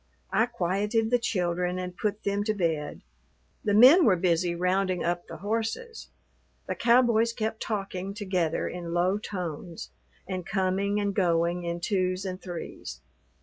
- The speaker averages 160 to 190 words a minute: No, average, 145 wpm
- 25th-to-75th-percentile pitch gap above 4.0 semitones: No, average, 3.2 semitones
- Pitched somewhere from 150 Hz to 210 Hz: Yes, high, 190 Hz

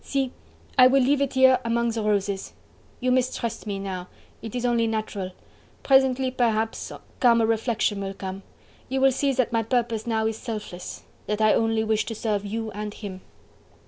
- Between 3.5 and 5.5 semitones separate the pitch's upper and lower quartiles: No, average, 3.1 semitones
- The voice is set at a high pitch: Yes, high, 225 Hz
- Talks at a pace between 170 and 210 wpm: Yes, average, 175 wpm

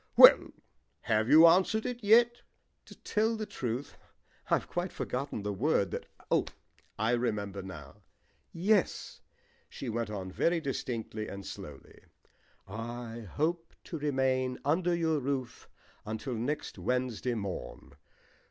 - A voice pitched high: No, low, 125 Hz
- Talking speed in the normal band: No, slow, 125 wpm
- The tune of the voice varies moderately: No, wide, 7.2 semitones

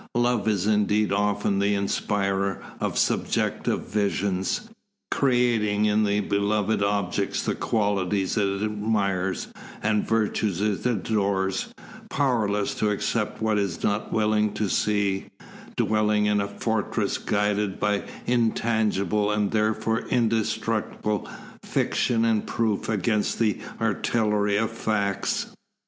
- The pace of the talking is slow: Yes, slow, 120 wpm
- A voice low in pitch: Yes, low, 105 Hz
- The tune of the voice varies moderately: No, narrow, 1.4 semitones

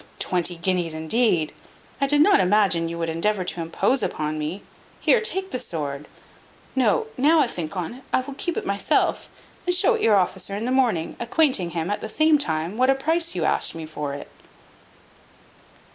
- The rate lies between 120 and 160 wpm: No, average, 190 wpm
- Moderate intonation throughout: No, wide, 8.4 semitones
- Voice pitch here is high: Yes, high, 200 Hz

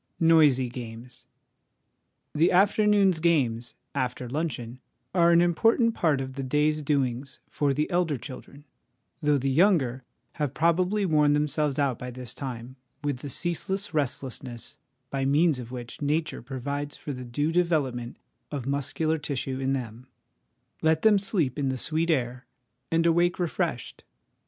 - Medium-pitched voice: Yes, medium, 145 Hz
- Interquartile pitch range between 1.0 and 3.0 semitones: No, average, 4.4 semitones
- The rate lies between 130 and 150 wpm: Yes, average, 145 wpm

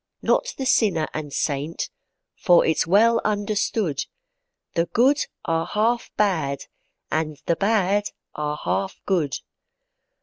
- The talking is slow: Yes, slow, 115 wpm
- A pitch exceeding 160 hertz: Yes, high, 190 Hz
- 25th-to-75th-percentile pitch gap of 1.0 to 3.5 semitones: No, wide, 5.5 semitones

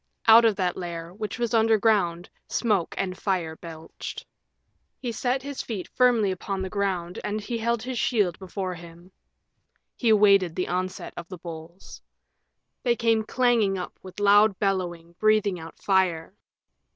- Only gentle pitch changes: No, average, 3.8 semitones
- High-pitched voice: Yes, high, 195 Hz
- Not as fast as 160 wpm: Yes, average, 150 wpm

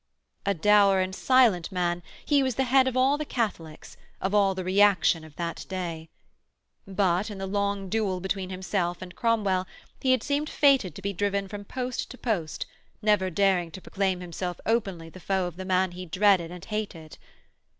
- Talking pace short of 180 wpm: No, average, 185 wpm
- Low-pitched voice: No, high, 195 Hz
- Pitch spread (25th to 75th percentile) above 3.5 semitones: No, average, 2.8 semitones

